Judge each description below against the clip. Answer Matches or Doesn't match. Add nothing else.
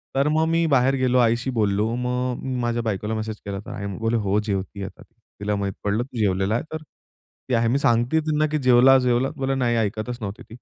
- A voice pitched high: Doesn't match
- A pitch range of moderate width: Matches